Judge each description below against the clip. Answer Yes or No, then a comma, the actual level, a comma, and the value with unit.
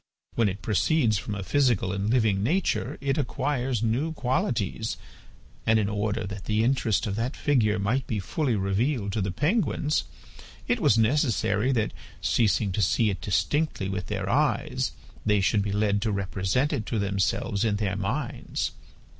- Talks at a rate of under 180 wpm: Yes, average, 165 wpm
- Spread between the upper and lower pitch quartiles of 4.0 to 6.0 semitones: Yes, average, 4.3 semitones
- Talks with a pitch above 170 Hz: No, low, 110 Hz